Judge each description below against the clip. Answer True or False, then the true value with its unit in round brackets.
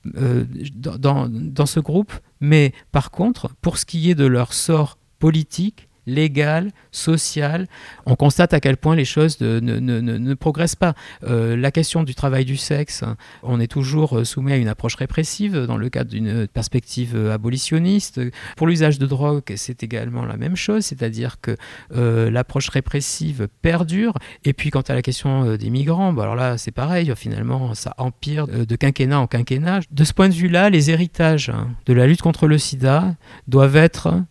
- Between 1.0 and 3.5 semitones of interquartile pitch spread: False (4.7 semitones)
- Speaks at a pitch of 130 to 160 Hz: True (140 Hz)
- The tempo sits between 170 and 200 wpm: True (185 wpm)